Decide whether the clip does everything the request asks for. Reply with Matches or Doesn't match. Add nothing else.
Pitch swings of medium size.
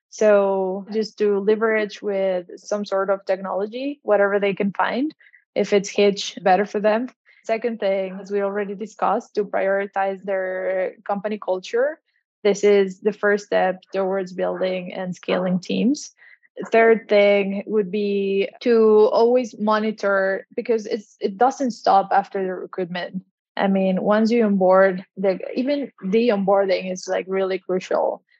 Doesn't match